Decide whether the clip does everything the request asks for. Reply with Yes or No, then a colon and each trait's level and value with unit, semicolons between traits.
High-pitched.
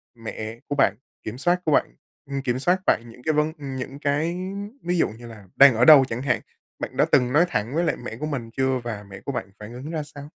No: low, 135 Hz